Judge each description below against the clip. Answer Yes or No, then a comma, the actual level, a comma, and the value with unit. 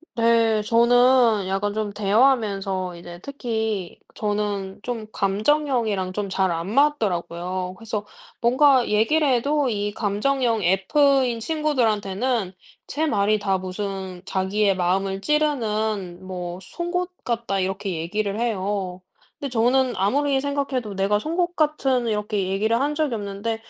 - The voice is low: No, high, 215 Hz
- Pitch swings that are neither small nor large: Yes, average, 4.8 semitones